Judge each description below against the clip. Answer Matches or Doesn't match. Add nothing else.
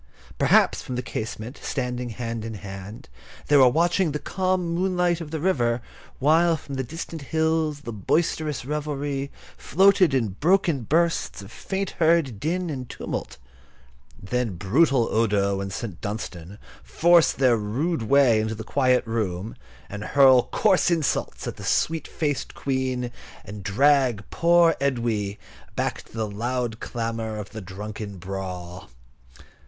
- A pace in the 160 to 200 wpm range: Doesn't match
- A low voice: Matches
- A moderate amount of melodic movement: Doesn't match